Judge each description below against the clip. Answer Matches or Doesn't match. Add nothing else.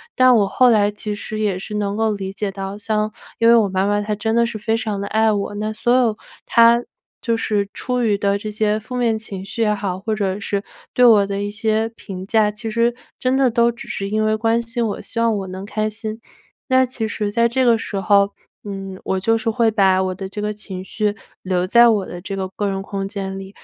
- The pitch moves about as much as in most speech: Doesn't match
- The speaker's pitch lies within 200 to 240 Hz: Matches